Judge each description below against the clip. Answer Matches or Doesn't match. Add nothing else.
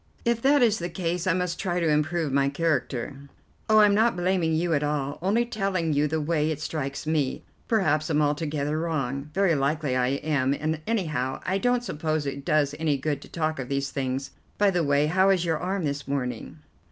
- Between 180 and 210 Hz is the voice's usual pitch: Doesn't match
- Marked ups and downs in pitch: Doesn't match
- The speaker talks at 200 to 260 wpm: Matches